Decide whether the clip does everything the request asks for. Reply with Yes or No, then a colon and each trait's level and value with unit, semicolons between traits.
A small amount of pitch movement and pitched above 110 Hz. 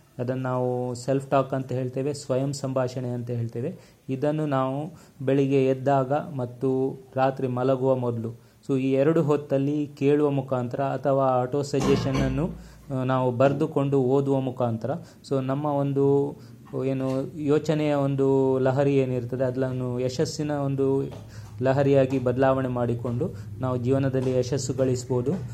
Yes: narrow, 1.7 semitones; low, 135 Hz